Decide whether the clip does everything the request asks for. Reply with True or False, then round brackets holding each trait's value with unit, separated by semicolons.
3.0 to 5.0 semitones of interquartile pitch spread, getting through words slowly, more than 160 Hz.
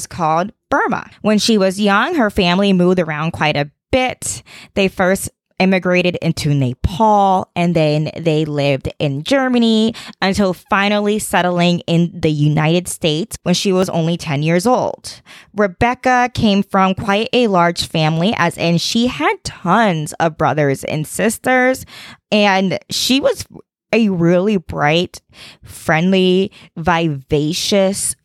True (4.3 semitones; 130 wpm; 185 Hz)